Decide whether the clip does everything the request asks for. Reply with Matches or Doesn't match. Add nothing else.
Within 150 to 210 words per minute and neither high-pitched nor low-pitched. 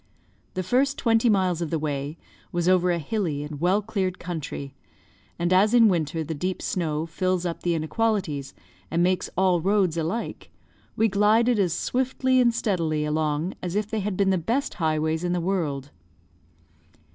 Matches